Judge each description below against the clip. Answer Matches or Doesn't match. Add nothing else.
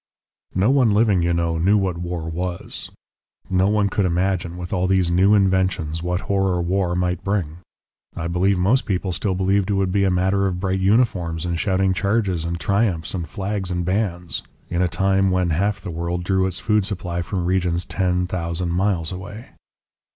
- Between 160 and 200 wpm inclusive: Matches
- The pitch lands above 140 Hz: Doesn't match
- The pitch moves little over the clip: Matches